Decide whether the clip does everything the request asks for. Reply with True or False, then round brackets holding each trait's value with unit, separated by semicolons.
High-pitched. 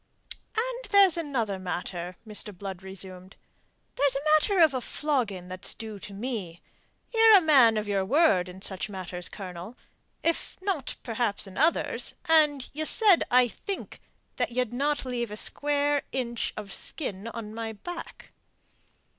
True (235 Hz)